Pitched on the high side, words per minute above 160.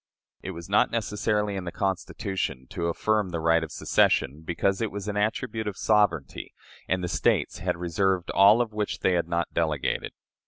No: very low, 95 Hz; average, 180 wpm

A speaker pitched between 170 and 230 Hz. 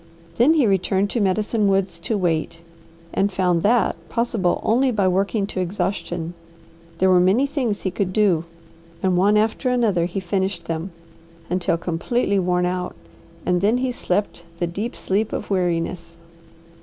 Yes: high, 190 Hz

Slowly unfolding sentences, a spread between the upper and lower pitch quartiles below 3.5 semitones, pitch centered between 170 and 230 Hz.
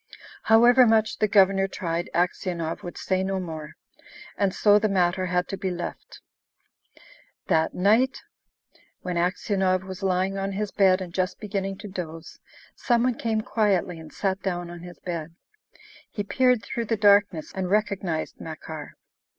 No: average, 155 wpm; average, 2.8 semitones; high, 190 Hz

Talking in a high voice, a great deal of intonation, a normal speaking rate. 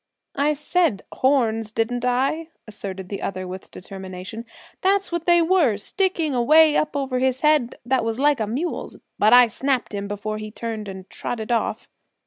Yes: high, 245 Hz; wide, 5.8 semitones; average, 170 wpm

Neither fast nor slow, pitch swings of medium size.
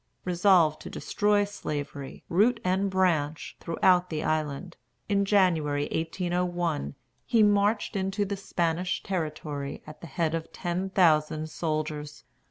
No: slow, 125 wpm; average, 3.8 semitones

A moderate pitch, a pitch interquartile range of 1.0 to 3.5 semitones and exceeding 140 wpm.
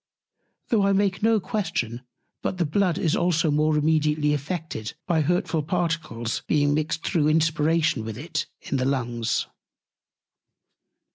No: medium, 155 Hz; average, 3.2 semitones; slow, 135 wpm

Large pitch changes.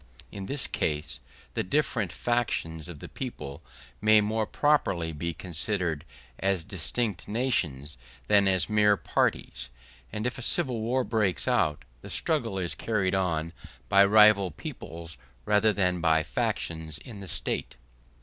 No: average, 4.9 semitones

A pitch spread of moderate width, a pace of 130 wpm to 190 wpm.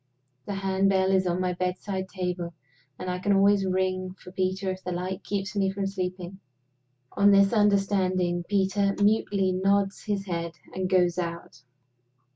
No: narrow, 1.4 semitones; average, 160 wpm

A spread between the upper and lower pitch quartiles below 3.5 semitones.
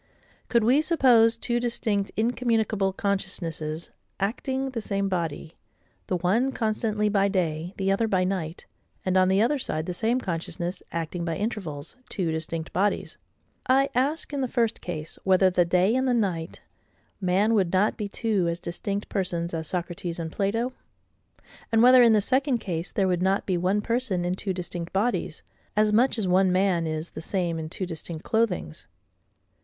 No: average, 4.6 semitones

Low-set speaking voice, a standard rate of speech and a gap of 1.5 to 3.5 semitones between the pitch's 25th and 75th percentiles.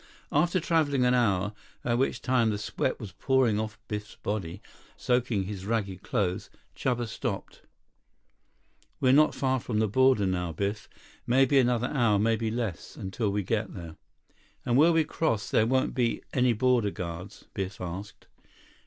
No: low, 115 Hz; average, 155 wpm; average, 4.2 semitones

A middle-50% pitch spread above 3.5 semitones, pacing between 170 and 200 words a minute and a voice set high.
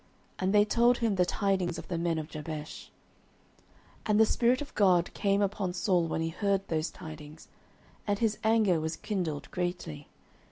No: average, 4.2 semitones; average, 175 wpm; medium, 180 Hz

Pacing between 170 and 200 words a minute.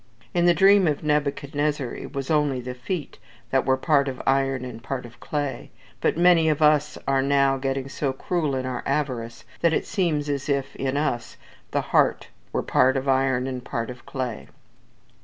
Yes: average, 190 wpm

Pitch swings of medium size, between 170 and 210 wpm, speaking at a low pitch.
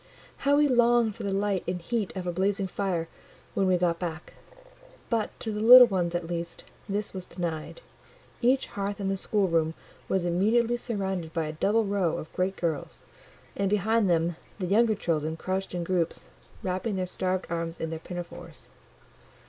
No: average, 3.4 semitones; average, 175 wpm; high, 190 Hz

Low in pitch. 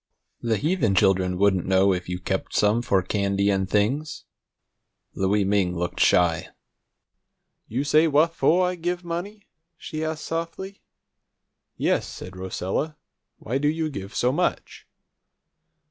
Yes: low, 110 Hz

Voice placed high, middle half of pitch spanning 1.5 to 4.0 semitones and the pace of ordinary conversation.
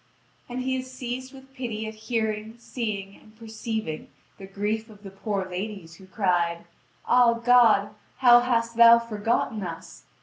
Yes: high, 220 Hz; average, 3.1 semitones; average, 155 wpm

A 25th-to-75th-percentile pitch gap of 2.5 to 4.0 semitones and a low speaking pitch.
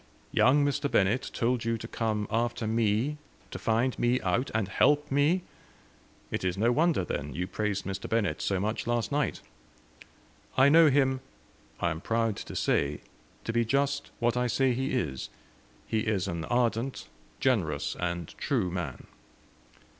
No: average, 5.2 semitones; low, 115 Hz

